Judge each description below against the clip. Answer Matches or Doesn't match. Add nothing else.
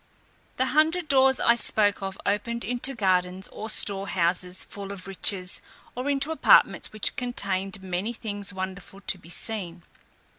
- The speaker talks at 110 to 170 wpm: Matches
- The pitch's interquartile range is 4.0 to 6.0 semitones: Matches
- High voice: Matches